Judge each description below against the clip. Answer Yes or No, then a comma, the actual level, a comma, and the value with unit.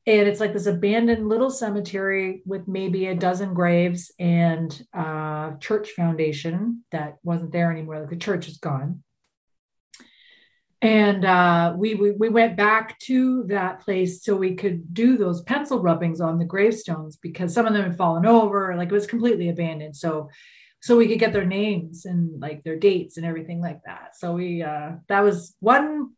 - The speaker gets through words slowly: No, average, 180 wpm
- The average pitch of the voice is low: No, medium, 185 Hz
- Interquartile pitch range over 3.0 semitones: Yes, average, 4.1 semitones